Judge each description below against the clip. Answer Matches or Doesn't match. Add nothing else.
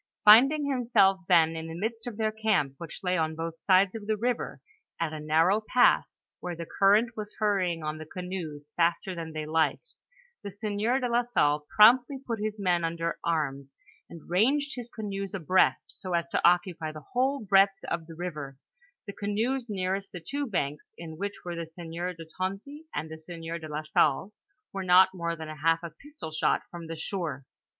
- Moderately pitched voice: Matches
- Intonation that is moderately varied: Matches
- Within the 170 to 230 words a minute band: Matches